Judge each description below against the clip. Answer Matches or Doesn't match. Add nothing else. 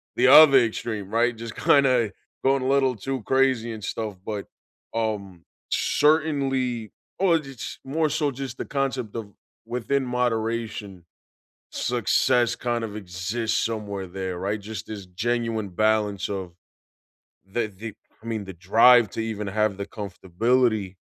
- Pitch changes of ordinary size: Matches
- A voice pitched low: Matches